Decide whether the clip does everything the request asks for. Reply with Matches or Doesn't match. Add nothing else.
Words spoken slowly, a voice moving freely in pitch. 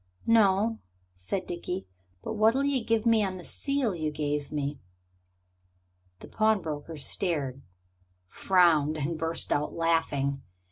Matches